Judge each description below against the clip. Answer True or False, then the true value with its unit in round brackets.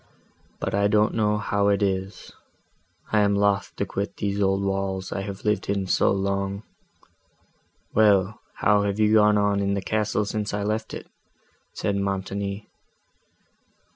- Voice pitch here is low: True (100 Hz)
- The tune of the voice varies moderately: False (1.2 semitones)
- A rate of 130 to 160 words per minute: True (150 wpm)